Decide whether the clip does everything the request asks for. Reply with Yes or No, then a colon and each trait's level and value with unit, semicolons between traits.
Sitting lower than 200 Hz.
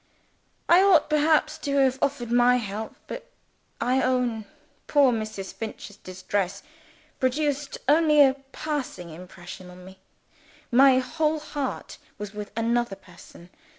No: very high, 250 Hz